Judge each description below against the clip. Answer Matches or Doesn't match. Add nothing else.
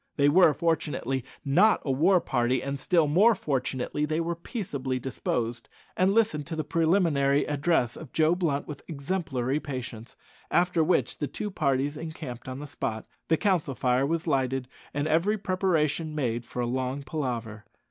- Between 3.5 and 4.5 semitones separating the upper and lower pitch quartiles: Matches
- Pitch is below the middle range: Doesn't match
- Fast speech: Doesn't match